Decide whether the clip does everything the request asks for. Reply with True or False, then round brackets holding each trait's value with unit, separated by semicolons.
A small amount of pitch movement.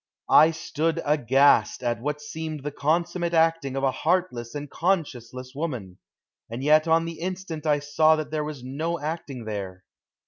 False (3.7 semitones)